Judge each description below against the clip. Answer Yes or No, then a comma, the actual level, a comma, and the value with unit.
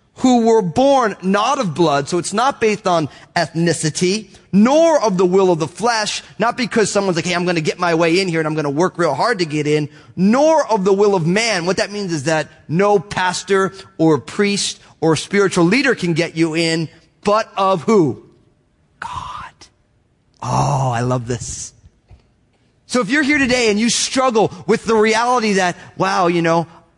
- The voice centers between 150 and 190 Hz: Yes, medium, 185 Hz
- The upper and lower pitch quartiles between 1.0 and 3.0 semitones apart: No, average, 4.8 semitones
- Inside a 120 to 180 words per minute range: No, average, 190 wpm